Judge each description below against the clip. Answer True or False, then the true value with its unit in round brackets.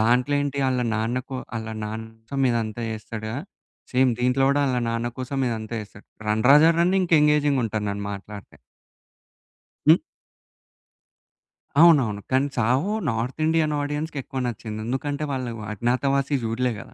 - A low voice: True (125 Hz)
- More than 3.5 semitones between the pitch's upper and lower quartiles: True (4.2 semitones)